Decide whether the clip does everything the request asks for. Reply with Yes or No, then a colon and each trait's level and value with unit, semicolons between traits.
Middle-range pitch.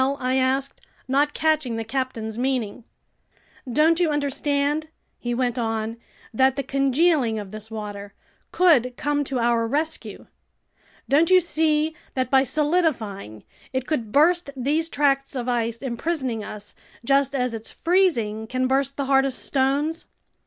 No: very high, 265 Hz